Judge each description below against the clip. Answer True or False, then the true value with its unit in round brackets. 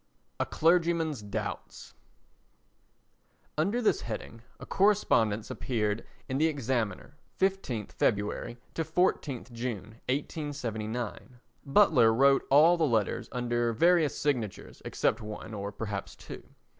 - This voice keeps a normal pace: False (110 wpm)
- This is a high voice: False (125 Hz)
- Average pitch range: False (6.2 semitones)